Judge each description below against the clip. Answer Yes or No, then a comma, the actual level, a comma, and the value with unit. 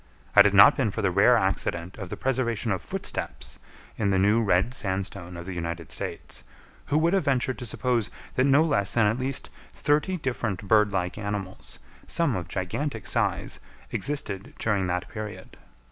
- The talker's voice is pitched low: Yes, low, 105 Hz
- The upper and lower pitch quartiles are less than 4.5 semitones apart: No, average, 5.1 semitones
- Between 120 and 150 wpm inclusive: No, average, 175 wpm